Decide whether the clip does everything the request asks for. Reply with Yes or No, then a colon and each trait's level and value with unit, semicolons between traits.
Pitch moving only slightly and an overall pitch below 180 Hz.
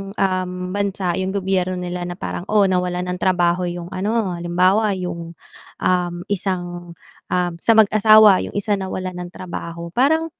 No: narrow, 2.1 semitones; medium, 185 Hz